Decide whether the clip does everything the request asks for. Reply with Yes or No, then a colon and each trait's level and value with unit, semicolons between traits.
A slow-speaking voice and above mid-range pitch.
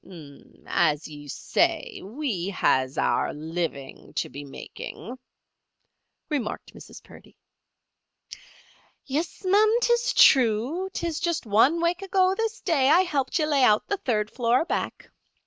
Yes: slow, 130 wpm; very high, 270 Hz